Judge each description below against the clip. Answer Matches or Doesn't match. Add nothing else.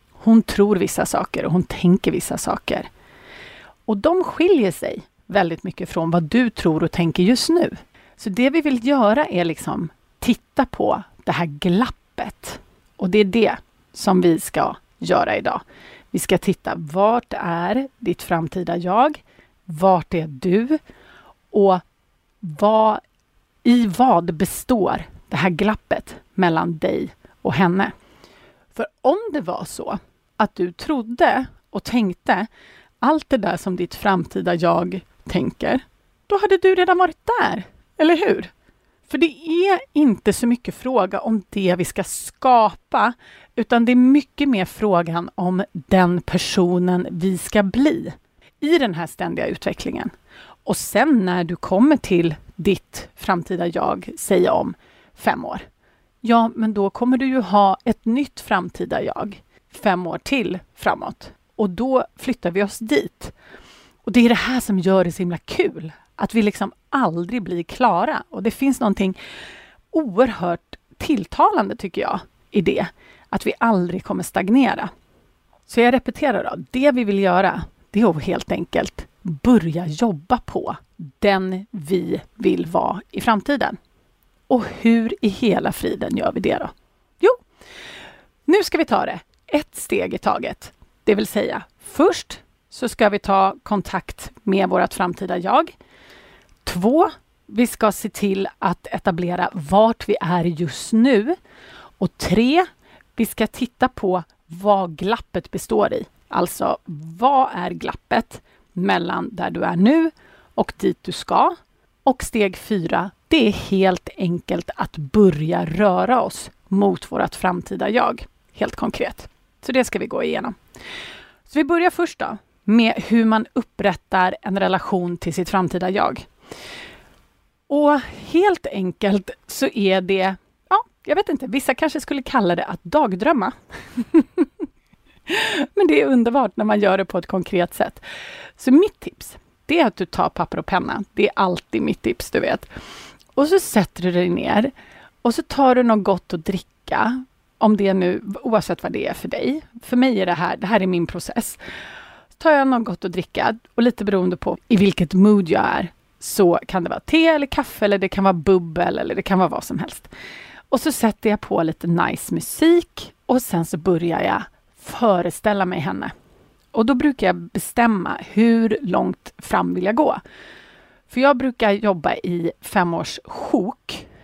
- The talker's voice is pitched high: Matches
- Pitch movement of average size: Doesn't match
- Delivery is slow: Doesn't match